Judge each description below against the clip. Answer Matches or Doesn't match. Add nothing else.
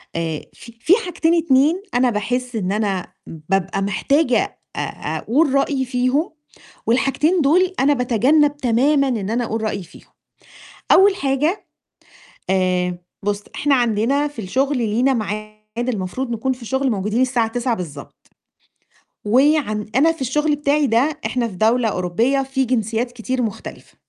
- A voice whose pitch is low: Doesn't match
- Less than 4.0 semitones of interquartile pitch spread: Doesn't match